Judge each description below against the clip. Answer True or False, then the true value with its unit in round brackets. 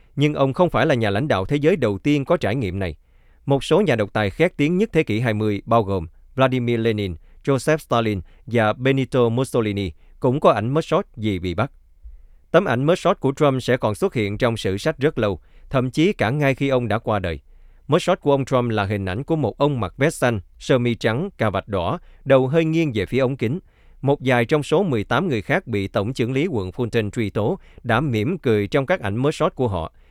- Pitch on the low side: True (120 Hz)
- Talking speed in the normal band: True (235 wpm)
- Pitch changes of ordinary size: False (5.7 semitones)